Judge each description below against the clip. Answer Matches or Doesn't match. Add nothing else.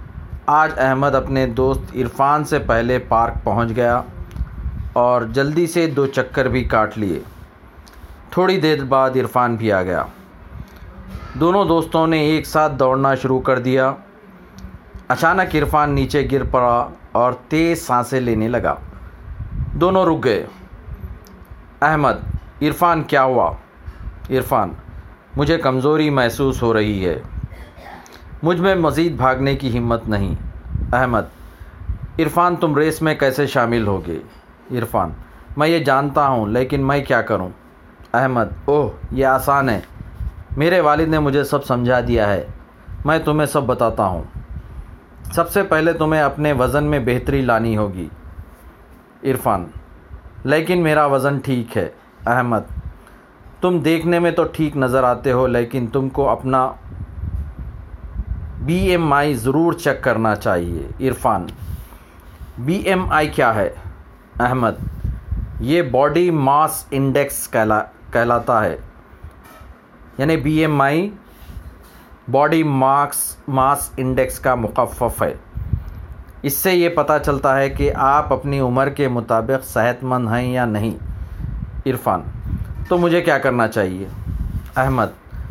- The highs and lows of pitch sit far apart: Matches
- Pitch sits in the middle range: Doesn't match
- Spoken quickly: Matches